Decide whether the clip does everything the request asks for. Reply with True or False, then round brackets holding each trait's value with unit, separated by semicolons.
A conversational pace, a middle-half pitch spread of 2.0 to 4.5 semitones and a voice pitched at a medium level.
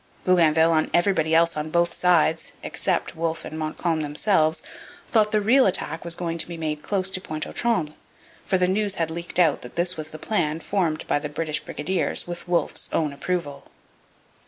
True (185 wpm; 2.7 semitones; 165 Hz)